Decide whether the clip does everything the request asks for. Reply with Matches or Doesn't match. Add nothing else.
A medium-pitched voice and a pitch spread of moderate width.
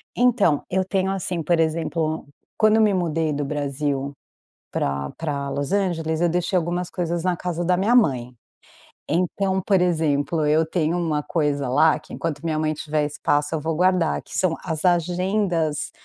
Matches